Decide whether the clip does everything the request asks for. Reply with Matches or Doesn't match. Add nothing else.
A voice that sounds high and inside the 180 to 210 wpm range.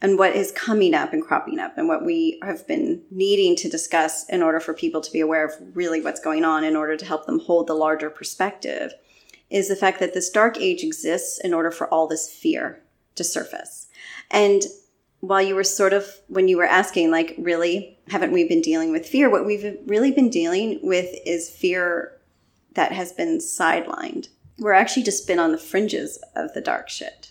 Matches